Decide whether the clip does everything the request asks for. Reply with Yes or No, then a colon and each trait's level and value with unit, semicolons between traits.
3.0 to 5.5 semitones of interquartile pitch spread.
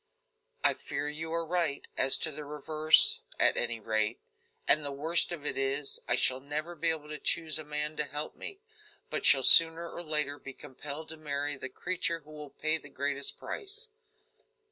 No: narrow, 2.4 semitones